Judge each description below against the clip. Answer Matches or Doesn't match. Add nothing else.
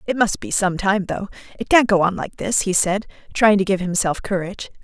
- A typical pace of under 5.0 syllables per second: Doesn't match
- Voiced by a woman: Matches